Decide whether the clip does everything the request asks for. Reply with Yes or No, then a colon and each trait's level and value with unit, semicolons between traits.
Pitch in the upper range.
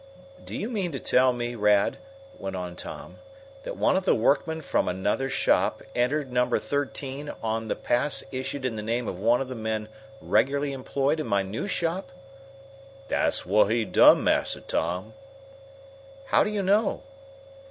No: low, 125 Hz